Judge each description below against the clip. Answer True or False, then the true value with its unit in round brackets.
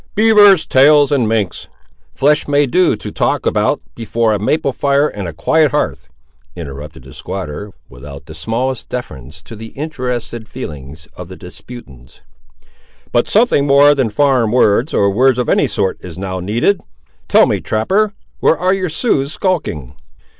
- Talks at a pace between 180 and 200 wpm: False (160 wpm)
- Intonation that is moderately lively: False (7.8 semitones)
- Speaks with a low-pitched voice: True (120 Hz)